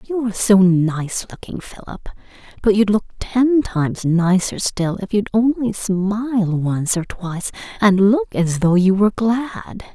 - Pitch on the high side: Yes, high, 200 Hz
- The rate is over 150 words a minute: Yes, average, 165 wpm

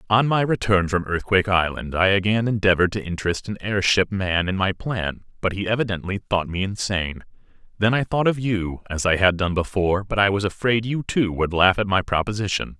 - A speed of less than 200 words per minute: No, fast, 205 wpm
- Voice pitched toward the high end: No, low, 100 Hz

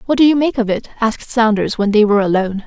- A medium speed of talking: No, fast, 270 wpm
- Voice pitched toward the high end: Yes, high, 225 Hz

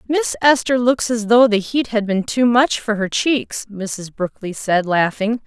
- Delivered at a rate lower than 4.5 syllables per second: Yes, 4.1 syllables/s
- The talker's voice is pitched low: No, high, 225 Hz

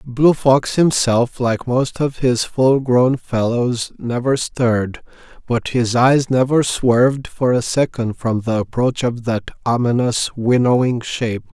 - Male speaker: Yes, male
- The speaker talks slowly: No, average, 145 wpm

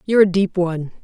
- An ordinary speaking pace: No, fast, 230 wpm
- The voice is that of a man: No, female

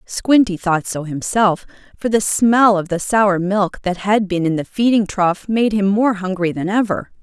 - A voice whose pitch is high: Yes, high, 200 Hz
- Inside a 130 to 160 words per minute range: No, average, 200 wpm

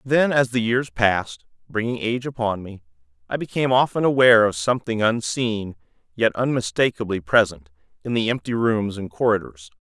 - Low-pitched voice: Yes, low, 110 Hz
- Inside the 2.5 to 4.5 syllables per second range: No, 5.5 syllables/s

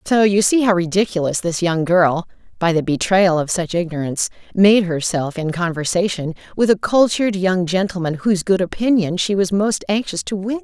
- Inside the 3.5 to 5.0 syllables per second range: No, 5.2 syllables/s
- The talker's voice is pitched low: No, medium, 185 Hz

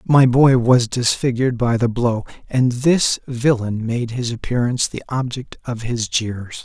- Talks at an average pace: Yes, average, 165 wpm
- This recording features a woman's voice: No, male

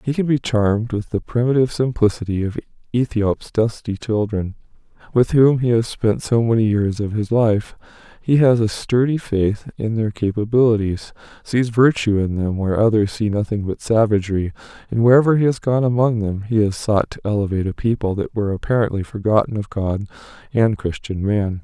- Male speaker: Yes, male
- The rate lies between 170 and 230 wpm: Yes, average, 180 wpm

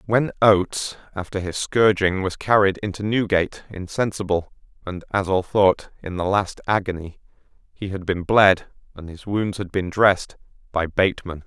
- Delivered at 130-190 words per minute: Yes, average, 155 wpm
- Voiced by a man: Yes, male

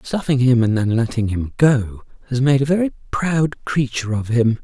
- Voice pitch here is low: Yes, low, 125 Hz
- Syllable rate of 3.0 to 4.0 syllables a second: No, 4.9 syllables/s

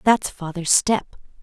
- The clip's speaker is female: Yes, female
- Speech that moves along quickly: No, slow, 125 wpm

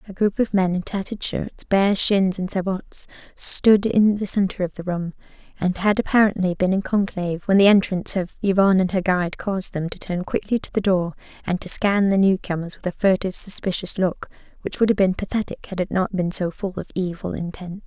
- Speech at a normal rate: No, fast, 220 wpm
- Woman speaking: Yes, female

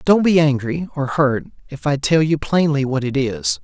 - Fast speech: No, average, 180 wpm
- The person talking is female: No, male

